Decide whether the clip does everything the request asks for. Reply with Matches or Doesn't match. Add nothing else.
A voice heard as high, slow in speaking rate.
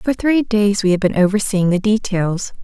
Doesn't match